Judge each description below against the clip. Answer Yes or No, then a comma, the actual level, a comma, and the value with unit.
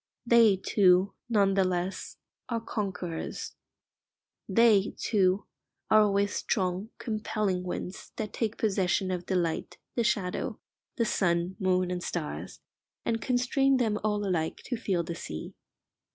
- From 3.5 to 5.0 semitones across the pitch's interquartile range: No, average, 3.1 semitones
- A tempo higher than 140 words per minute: No, slow, 135 wpm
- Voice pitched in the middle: No, high, 195 Hz